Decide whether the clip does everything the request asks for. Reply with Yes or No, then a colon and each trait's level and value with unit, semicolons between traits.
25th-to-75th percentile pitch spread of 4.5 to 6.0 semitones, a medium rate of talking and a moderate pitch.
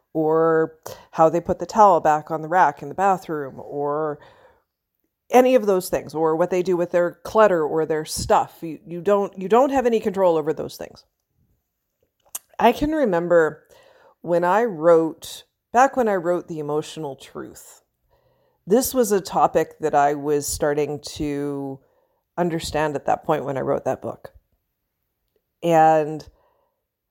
Yes: average, 5.2 semitones; average, 155 wpm; medium, 170 Hz